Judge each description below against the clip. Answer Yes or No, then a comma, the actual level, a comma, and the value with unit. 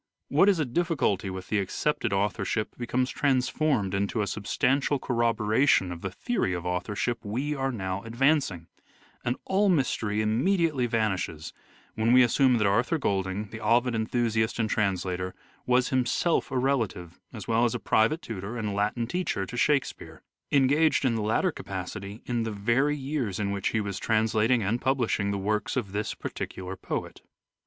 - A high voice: No, low, 115 Hz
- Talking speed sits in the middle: Yes, average, 170 wpm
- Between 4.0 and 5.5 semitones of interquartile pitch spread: Yes, average, 4.4 semitones